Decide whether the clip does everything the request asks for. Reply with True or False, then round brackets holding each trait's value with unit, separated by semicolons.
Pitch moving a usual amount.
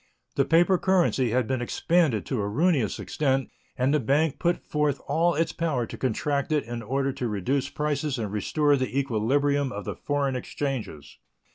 True (3.6 semitones)